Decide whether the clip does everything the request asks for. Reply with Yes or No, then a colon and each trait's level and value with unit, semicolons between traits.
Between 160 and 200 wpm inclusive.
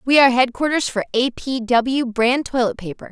Yes: average, 190 wpm